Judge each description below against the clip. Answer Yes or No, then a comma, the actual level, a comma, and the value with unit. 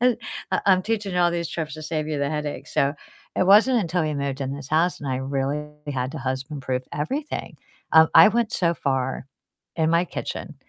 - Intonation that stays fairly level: No, average, 4.3 semitones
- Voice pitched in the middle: Yes, medium, 155 Hz